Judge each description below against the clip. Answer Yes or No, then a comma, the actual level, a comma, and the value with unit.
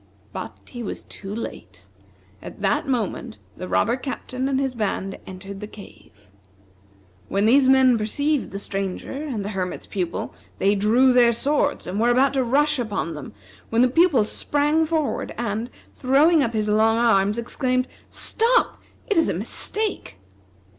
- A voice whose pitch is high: Yes, high, 235 Hz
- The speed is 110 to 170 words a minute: Yes, average, 160 wpm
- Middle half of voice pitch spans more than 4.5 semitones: Yes, average, 5.2 semitones